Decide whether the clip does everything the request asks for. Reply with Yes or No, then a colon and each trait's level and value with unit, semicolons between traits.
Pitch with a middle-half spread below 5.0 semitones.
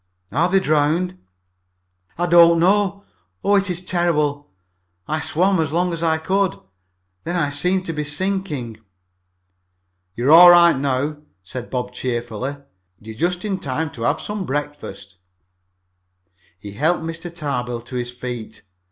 No: wide, 5.6 semitones